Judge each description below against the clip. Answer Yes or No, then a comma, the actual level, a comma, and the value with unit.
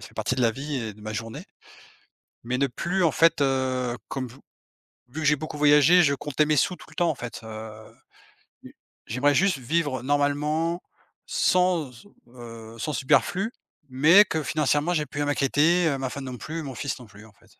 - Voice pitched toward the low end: No, medium, 145 Hz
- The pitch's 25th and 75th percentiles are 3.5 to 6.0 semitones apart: Yes, average, 4.0 semitones